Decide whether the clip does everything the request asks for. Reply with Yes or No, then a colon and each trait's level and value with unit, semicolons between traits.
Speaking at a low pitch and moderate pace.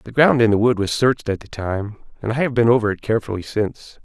No: low, 110 Hz; fast, 265 wpm